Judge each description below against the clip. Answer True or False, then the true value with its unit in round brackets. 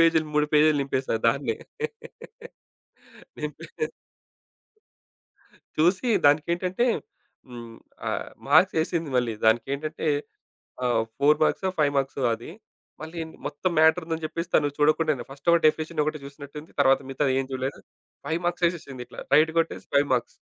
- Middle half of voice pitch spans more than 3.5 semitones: False (3.1 semitones)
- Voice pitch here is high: False (150 Hz)